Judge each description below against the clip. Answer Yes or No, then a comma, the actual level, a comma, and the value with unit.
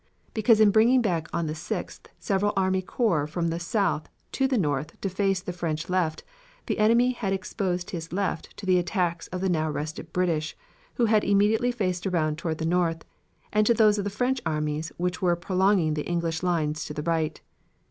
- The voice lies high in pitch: No, medium, 180 Hz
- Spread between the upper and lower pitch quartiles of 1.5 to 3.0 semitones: No, average, 4.0 semitones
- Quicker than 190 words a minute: Yes, average, 200 wpm